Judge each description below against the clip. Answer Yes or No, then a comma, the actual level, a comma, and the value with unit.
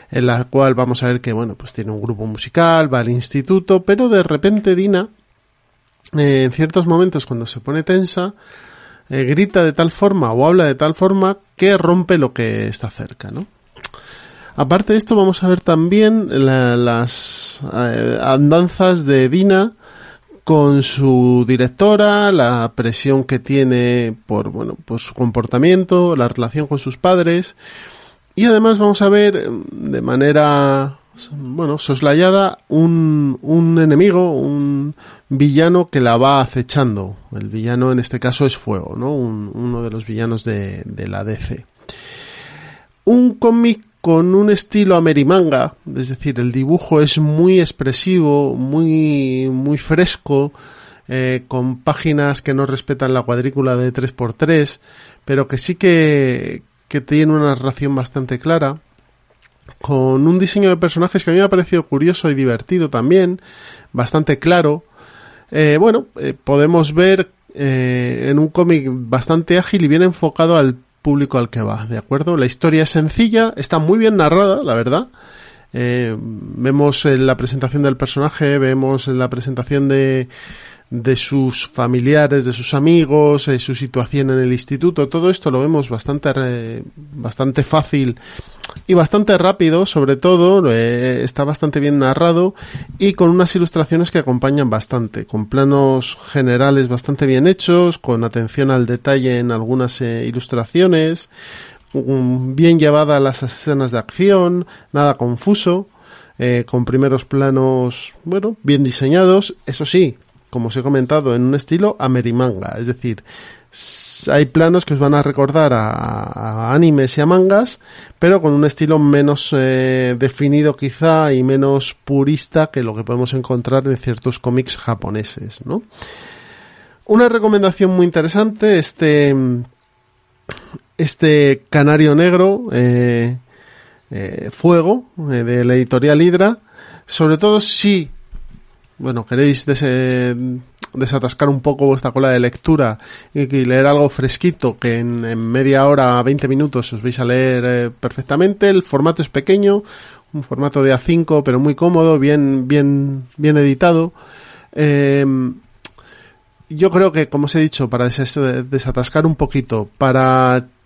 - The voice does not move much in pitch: No, average, 4.8 semitones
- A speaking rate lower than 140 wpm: No, average, 145 wpm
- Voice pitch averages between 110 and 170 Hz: Yes, medium, 140 Hz